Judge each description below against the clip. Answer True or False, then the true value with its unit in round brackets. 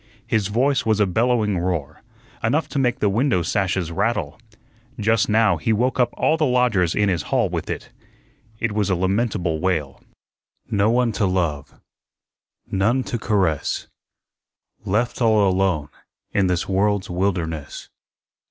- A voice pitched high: False (100 Hz)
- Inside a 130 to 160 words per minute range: True (145 wpm)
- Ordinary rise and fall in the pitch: True (4.1 semitones)